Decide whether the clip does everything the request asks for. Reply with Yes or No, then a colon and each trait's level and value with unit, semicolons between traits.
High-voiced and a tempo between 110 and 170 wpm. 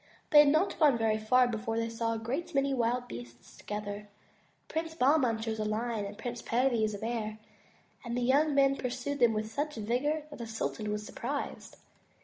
No: high, 235 Hz; average, 190 wpm